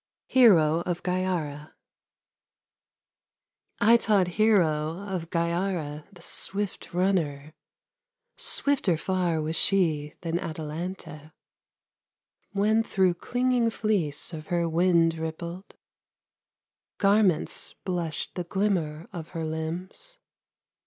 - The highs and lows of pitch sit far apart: No, average, 3.6 semitones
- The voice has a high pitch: No, medium, 175 Hz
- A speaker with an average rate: No, slow, 90 wpm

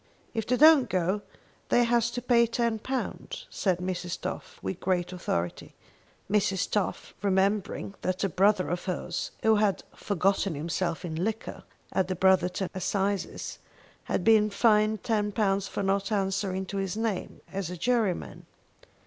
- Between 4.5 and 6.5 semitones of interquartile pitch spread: No, average, 2.9 semitones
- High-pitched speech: Yes, high, 195 Hz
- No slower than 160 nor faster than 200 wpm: No, average, 145 wpm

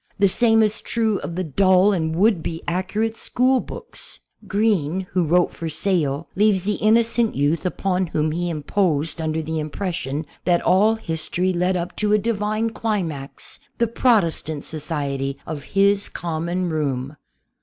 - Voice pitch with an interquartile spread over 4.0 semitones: Yes, average, 4.7 semitones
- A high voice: No, medium, 180 Hz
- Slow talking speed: No, average, 160 wpm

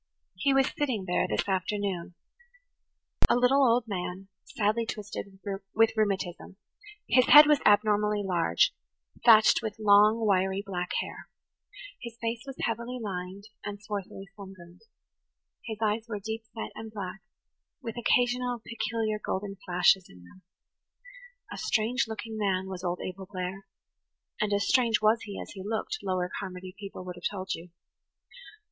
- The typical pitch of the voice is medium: No, high, 205 Hz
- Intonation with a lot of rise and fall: No, average, 3.3 semitones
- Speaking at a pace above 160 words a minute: No, average, 145 wpm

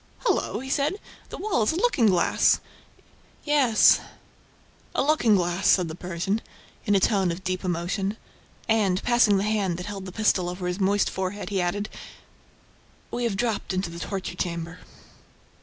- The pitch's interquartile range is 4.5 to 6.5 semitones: No, average, 3.7 semitones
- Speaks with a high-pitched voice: Yes, high, 195 Hz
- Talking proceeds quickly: No, average, 165 wpm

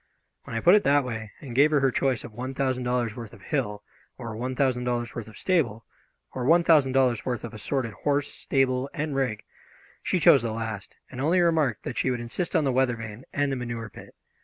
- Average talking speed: No, fast, 230 wpm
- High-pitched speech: No, low, 125 Hz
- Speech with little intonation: No, average, 3.1 semitones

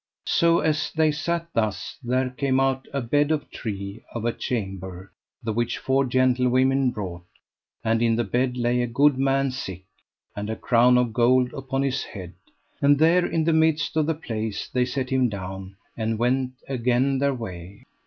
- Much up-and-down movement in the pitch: No, average, 3.5 semitones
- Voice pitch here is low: Yes, low, 125 Hz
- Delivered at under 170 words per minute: No, average, 180 wpm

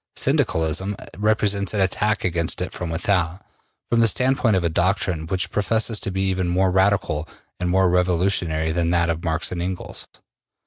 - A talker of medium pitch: No, very low, 90 Hz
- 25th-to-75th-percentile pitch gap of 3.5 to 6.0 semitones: No, average, 2.9 semitones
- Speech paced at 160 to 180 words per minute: Yes, average, 170 wpm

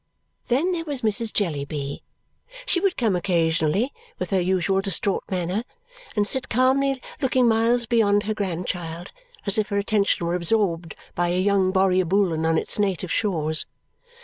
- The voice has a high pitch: Yes, high, 195 Hz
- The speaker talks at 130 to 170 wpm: Yes, average, 150 wpm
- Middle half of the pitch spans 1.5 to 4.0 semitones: No, average, 4.5 semitones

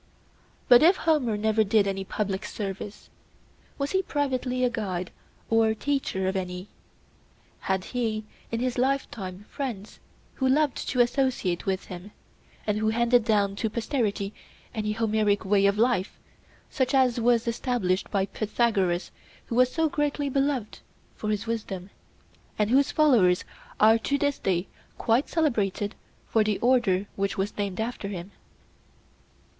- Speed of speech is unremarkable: Yes, average, 145 wpm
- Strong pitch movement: No, average, 4.2 semitones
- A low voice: No, high, 220 Hz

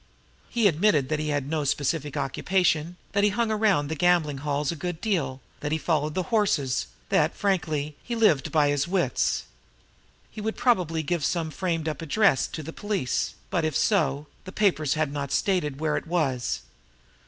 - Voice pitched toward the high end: No, medium, 160 Hz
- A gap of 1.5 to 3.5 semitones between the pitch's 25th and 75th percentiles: No, average, 4.5 semitones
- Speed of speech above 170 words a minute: Yes, average, 180 wpm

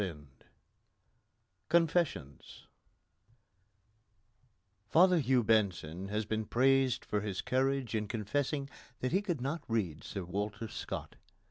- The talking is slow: Yes, slow, 110 wpm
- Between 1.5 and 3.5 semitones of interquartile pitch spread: No, average, 5.1 semitones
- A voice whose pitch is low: Yes, low, 115 Hz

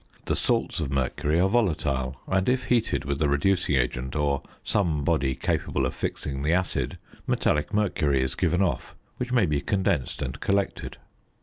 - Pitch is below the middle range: Yes, very low, 75 Hz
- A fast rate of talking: No, average, 170 wpm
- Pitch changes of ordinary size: No, wide, 5.8 semitones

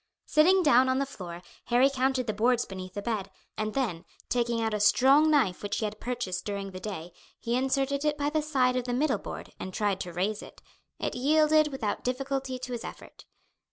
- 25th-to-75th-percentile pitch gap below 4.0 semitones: No, average, 4.8 semitones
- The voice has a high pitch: Yes, high, 245 Hz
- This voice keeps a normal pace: No, fast, 210 wpm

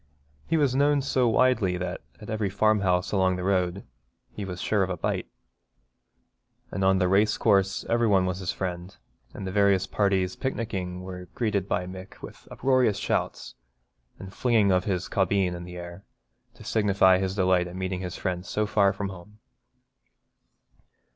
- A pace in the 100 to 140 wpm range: No, average, 175 wpm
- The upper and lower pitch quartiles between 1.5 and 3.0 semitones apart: Yes, narrow, 2.4 semitones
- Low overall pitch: Yes, very low, 95 Hz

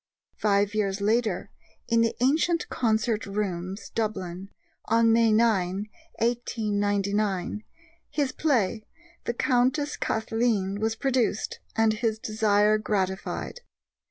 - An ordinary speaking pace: No, slow, 100 wpm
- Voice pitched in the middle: No, high, 215 Hz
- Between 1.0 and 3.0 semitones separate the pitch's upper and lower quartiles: Yes, narrow, 2.4 semitones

